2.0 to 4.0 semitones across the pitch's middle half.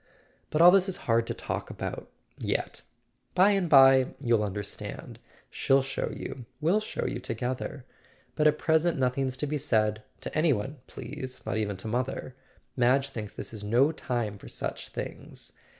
No: average, 4.9 semitones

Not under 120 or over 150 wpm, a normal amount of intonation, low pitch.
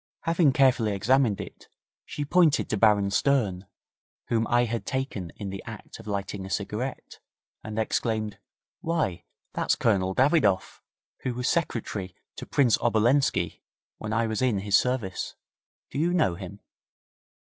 Yes: average, 145 wpm; average, 4.8 semitones; low, 110 Hz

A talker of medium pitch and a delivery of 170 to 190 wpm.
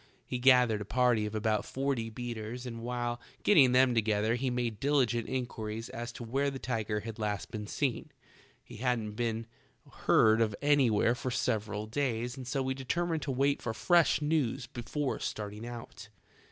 No: low, 120 Hz; average, 175 wpm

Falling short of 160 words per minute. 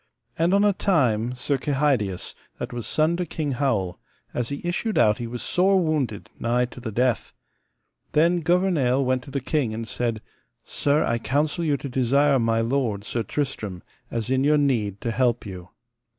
No: average, 180 wpm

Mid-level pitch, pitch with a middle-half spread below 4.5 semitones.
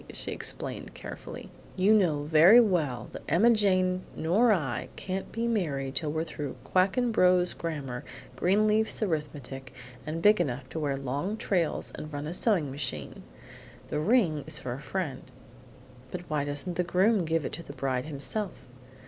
No: medium, 165 Hz; average, 5.1 semitones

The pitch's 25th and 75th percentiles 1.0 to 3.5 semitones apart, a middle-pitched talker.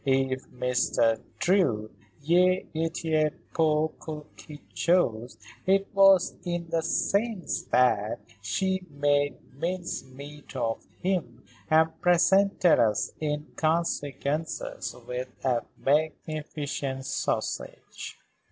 No: average, 4.8 semitones; medium, 155 Hz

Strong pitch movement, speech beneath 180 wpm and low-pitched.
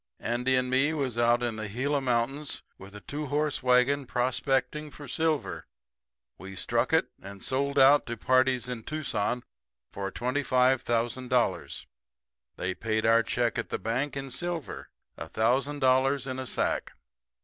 No: average, 3.0 semitones; average, 150 wpm; low, 130 Hz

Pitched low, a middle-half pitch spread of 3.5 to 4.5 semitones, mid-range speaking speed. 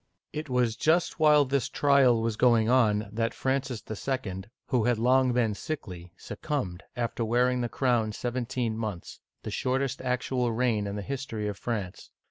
No: low, 120 Hz; average, 3.0 semitones; average, 160 wpm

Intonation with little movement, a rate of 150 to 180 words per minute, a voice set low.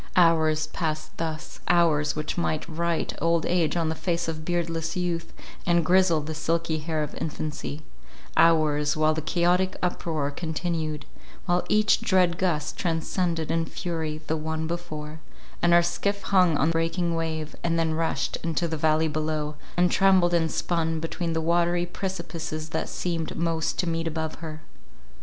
No: narrow, 1.7 semitones; average, 160 wpm; medium, 165 Hz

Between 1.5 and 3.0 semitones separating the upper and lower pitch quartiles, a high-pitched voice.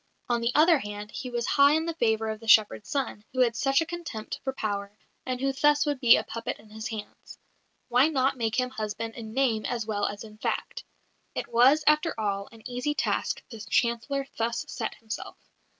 No: average, 3.9 semitones; high, 235 Hz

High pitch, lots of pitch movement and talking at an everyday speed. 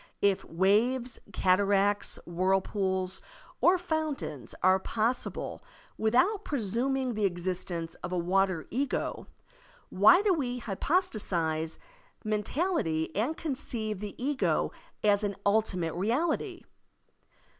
No: high, 210 Hz; wide, 5.7 semitones; slow, 100 wpm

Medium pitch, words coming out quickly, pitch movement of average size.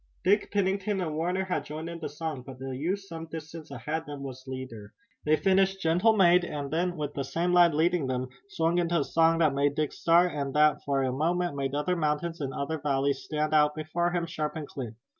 Yes: medium, 155 Hz; fast, 225 wpm; average, 3.5 semitones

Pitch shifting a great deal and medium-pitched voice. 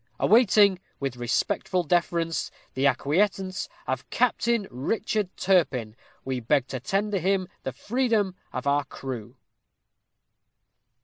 Yes: wide, 7.2 semitones; medium, 175 Hz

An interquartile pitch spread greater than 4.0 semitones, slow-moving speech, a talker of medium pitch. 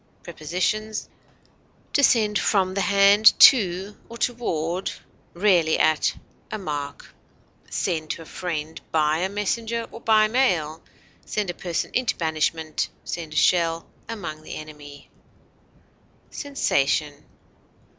Yes: average, 5.3 semitones; slow, 115 wpm; medium, 180 Hz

